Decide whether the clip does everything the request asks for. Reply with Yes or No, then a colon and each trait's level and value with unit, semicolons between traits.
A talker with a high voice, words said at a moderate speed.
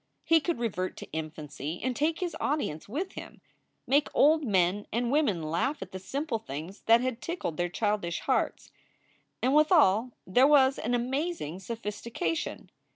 Yes: high, 235 Hz; average, 155 wpm